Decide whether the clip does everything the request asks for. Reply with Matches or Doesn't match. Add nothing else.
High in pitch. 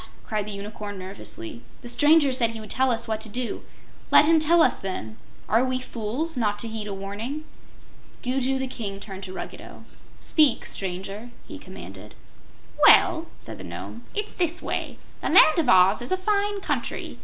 Matches